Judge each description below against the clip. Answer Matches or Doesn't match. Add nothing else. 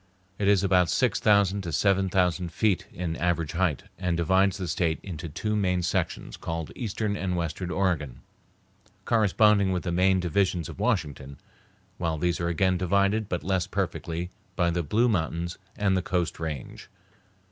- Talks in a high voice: Doesn't match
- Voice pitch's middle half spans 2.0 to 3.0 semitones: Matches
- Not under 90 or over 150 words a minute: Doesn't match